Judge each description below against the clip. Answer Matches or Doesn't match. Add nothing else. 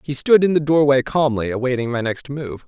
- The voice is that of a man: Matches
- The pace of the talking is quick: Matches